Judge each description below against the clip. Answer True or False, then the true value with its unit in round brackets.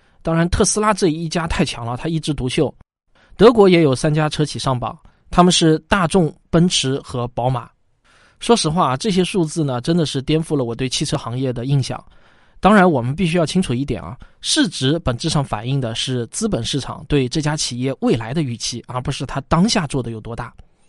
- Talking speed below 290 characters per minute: False (300 characters per minute)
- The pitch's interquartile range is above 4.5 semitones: True (5.1 semitones)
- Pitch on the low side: False (150 Hz)